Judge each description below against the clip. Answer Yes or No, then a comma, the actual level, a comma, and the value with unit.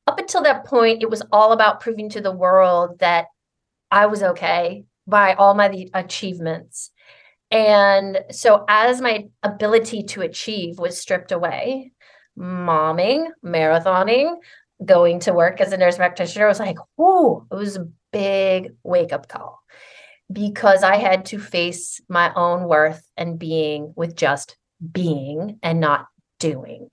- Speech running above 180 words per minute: No, average, 145 wpm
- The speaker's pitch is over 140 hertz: Yes, high, 190 Hz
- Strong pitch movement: No, average, 3.7 semitones